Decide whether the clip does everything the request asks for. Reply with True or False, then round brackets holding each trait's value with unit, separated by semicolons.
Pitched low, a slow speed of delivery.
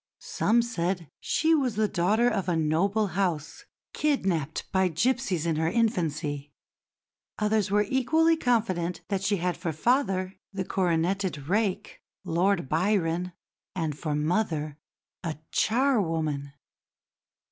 False (185 Hz; 120 wpm)